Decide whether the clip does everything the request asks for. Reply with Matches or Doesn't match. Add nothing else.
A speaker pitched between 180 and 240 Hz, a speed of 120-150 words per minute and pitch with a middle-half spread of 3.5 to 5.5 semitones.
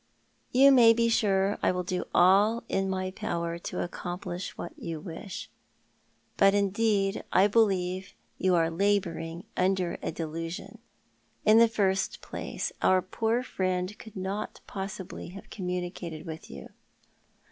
Doesn't match